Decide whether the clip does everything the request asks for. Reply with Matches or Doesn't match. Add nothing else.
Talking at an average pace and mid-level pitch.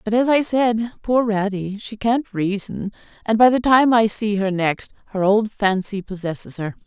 Doesn't match